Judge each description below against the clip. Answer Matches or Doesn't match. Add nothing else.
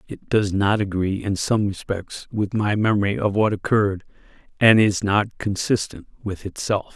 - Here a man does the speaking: Matches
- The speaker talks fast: Doesn't match